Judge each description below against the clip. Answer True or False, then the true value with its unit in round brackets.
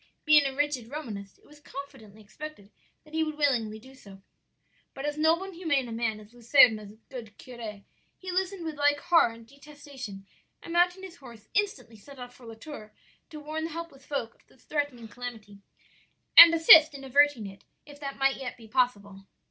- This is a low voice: False (270 Hz)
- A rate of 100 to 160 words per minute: False (190 wpm)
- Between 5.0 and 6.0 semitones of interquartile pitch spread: True (5.3 semitones)